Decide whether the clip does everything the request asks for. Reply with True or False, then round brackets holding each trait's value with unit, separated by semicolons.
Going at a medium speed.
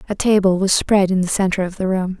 False (275 wpm)